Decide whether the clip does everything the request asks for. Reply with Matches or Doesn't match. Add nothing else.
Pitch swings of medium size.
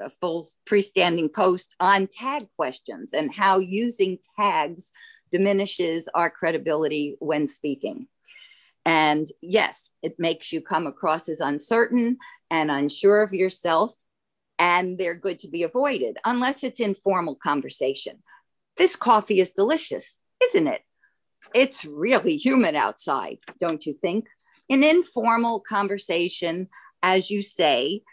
Doesn't match